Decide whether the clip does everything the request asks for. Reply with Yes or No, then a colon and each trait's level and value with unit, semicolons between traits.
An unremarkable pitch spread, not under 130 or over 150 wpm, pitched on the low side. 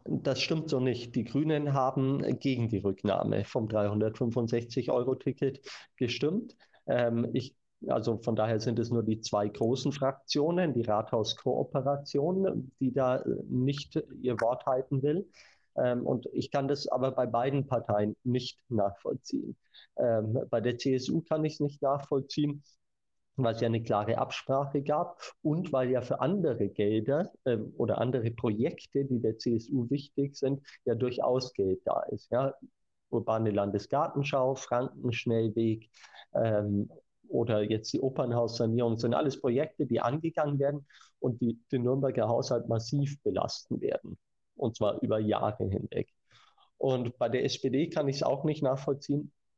Yes: average, 3.5 semitones; average, 145 wpm; low, 125 Hz